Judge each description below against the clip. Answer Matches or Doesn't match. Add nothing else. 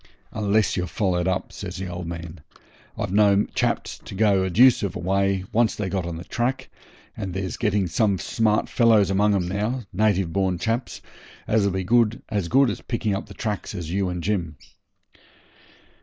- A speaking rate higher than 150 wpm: Matches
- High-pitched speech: Doesn't match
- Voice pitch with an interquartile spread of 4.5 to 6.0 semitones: Doesn't match